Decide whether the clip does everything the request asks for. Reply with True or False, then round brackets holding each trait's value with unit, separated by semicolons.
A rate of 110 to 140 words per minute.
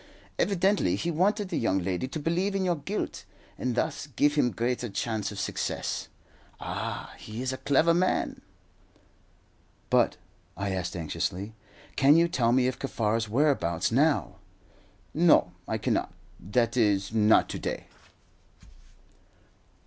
True (135 wpm)